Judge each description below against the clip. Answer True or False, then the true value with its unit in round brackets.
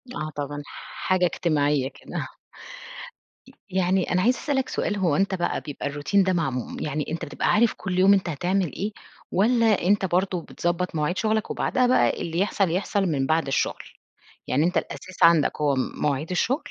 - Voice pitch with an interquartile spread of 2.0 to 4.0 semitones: False (4.5 semitones)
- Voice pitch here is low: False (180 Hz)